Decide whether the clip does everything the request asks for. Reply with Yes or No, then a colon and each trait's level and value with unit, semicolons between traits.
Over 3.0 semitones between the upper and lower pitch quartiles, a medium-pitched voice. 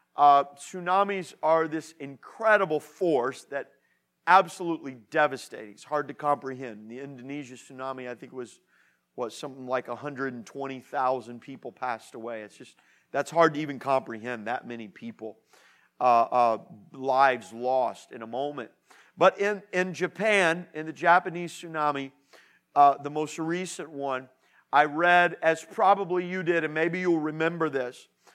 Yes: average, 4.6 semitones; medium, 145 Hz